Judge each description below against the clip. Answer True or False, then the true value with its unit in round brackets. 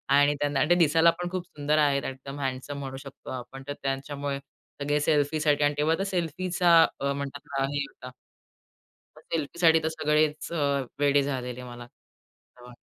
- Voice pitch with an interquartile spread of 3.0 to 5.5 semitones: False (2.6 semitones)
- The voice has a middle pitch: True (145 Hz)